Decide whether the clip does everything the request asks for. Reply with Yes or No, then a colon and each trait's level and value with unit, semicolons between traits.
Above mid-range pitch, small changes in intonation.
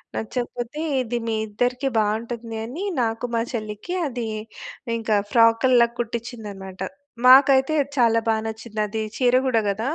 Yes: high, 230 Hz; narrow, 2.1 semitones